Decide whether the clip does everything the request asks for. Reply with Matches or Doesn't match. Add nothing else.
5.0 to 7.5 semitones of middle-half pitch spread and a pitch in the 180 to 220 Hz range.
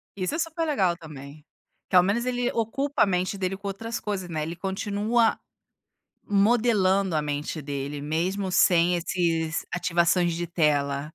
Doesn't match